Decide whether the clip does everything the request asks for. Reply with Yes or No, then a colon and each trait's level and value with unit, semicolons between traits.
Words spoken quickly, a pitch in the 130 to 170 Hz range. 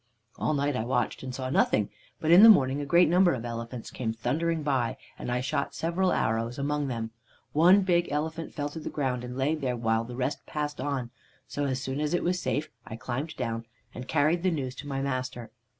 Yes: fast, 220 wpm; medium, 140 Hz